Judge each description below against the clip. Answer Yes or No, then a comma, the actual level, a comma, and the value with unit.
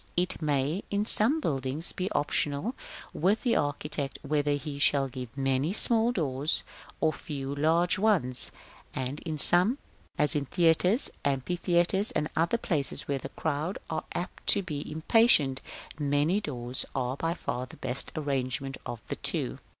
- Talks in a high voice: No, medium, 150 Hz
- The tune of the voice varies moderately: Yes, average, 4.6 semitones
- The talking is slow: No, average, 150 wpm